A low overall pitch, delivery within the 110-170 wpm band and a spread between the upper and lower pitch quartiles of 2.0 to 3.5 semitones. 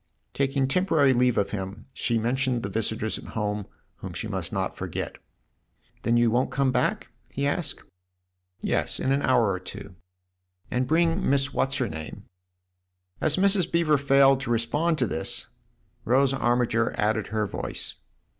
No: low, 125 Hz; average, 165 wpm; average, 4.1 semitones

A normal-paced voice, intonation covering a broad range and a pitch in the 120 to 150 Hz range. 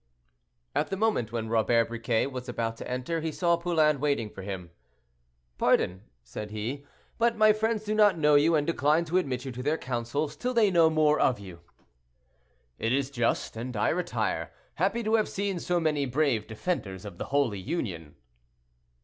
Yes: average, 185 wpm; wide, 6.8 semitones; medium, 140 Hz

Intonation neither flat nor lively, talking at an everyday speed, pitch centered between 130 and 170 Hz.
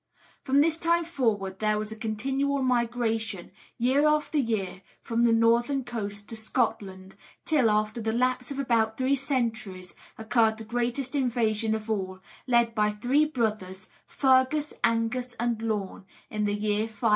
No: average, 3.3 semitones; average, 155 wpm; high, 230 Hz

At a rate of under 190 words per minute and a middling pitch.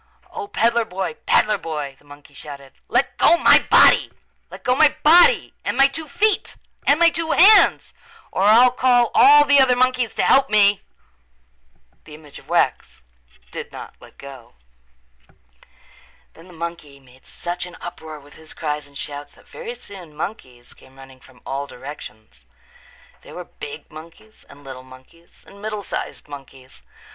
Yes: average, 165 wpm; medium, 170 Hz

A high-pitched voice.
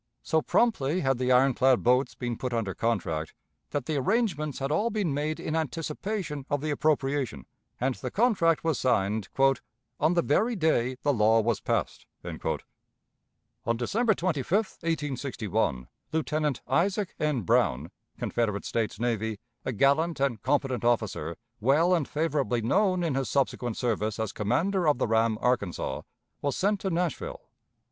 No: low, 135 Hz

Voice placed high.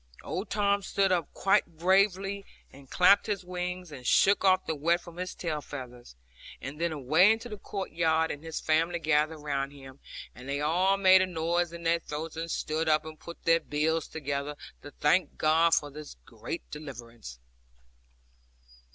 No: medium, 165 Hz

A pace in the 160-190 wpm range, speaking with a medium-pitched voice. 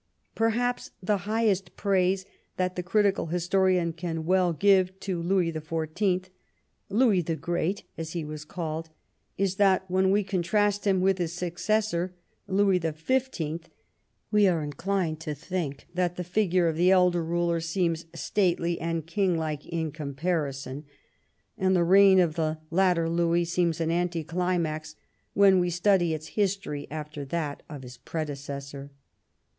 No: average, 150 wpm; medium, 175 Hz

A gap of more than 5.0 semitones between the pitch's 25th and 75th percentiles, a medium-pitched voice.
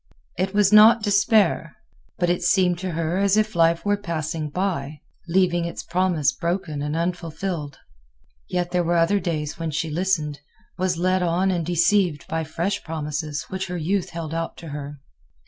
No: average, 2.9 semitones; medium, 175 Hz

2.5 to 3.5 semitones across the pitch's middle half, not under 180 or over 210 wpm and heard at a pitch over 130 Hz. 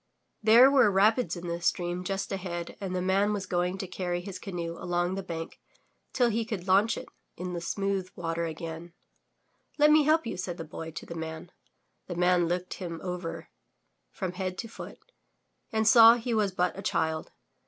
Yes: average, 2.9 semitones; average, 185 wpm; medium, 185 Hz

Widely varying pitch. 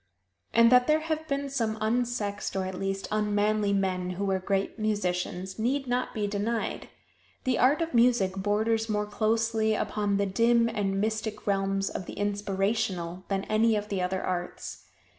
No: average, 2.9 semitones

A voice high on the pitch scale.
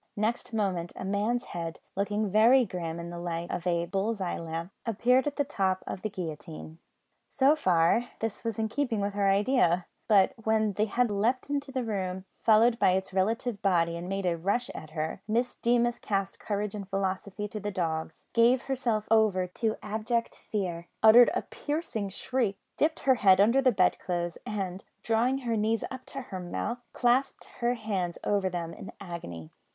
Yes: high, 205 Hz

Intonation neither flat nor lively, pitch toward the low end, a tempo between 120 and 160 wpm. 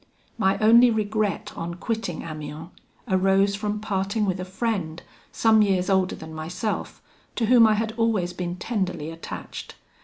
No: average, 3.6 semitones; high, 195 Hz; average, 150 wpm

